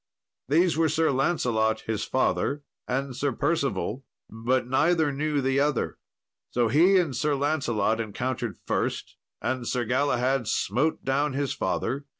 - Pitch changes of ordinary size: Yes, average, 3.4 semitones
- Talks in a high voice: No, low, 135 Hz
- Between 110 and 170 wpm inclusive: Yes, average, 140 wpm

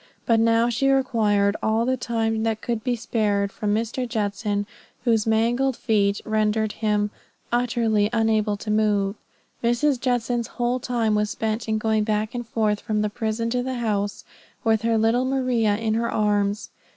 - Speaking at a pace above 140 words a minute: Yes, average, 165 wpm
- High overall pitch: Yes, high, 225 Hz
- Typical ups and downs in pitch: No, narrow, 2.0 semitones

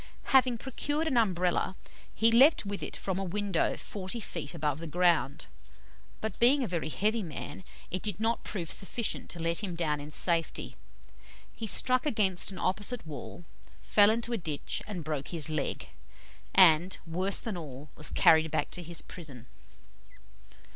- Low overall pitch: No, medium, 185 Hz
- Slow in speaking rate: No, average, 165 wpm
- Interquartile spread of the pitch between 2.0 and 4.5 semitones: No, average, 5.2 semitones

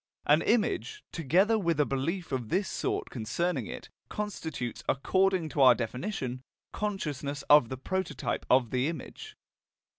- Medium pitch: Yes, medium, 155 Hz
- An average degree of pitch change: No, wide, 6.5 semitones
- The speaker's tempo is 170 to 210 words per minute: No, average, 140 wpm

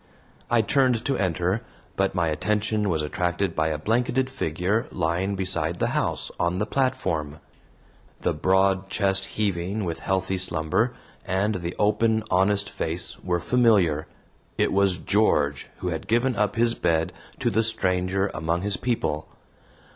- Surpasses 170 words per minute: No, average, 145 wpm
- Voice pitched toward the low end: Yes, very low, 95 Hz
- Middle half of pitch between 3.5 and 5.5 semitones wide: Yes, average, 4.0 semitones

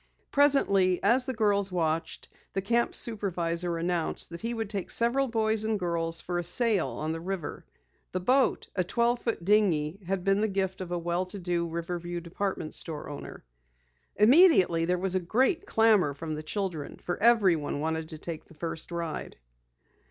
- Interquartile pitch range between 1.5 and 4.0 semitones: No, average, 4.4 semitones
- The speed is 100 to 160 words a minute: No, average, 175 wpm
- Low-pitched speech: No, medium, 185 Hz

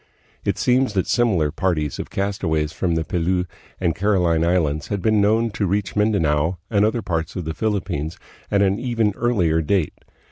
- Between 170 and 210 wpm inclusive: Yes, average, 175 wpm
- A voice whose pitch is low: Yes, very low, 95 Hz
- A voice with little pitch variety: No, average, 4.3 semitones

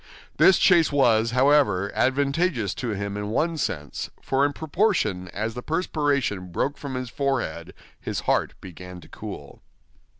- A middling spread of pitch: No, wide, 6.3 semitones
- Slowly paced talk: No, average, 145 wpm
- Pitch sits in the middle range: No, low, 130 Hz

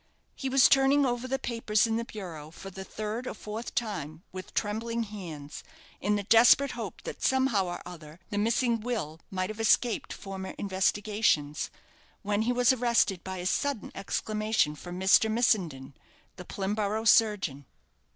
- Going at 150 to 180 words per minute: Yes, average, 160 wpm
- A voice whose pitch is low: No, high, 210 Hz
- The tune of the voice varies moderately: Yes, average, 3.9 semitones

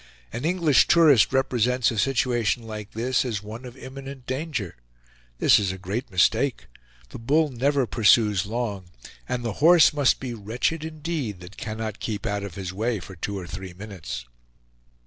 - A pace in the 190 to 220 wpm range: No, average, 165 wpm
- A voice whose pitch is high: No, low, 115 Hz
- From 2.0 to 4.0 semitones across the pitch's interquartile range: No, average, 4.7 semitones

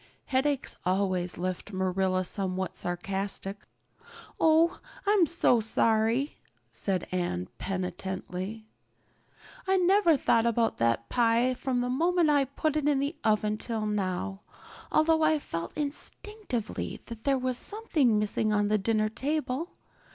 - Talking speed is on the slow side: Yes, slow, 130 wpm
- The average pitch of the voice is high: Yes, high, 225 Hz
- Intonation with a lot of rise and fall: Yes, wide, 7.1 semitones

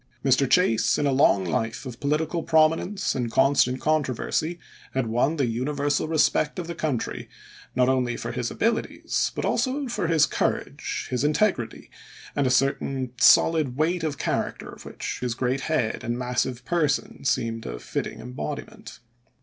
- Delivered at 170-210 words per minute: No, average, 160 wpm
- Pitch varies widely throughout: No, average, 4.1 semitones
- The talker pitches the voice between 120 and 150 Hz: Yes, low, 135 Hz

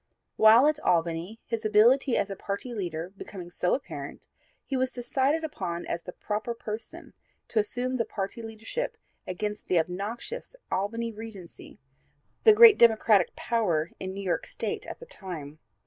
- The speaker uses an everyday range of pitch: Yes, average, 4.6 semitones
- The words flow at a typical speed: Yes, average, 155 wpm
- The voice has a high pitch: Yes, high, 215 Hz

